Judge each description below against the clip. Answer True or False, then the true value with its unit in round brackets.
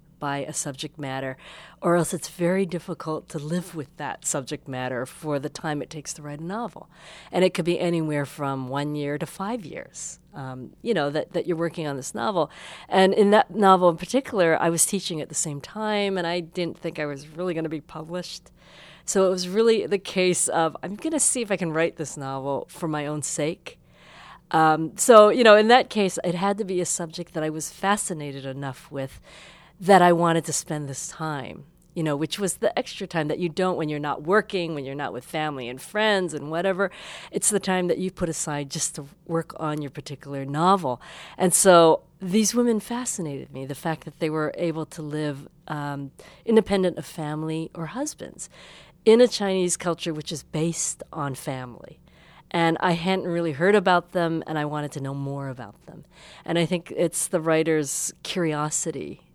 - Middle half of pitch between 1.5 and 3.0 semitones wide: False (3.6 semitones)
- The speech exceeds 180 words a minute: True (205 wpm)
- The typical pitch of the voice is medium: True (165 Hz)